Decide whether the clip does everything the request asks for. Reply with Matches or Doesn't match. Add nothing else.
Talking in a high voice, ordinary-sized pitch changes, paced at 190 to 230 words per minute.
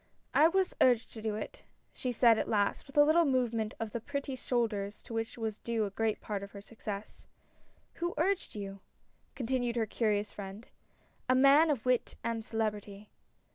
Matches